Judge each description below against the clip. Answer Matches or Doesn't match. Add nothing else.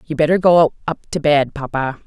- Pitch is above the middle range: Doesn't match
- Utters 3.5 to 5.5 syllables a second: Matches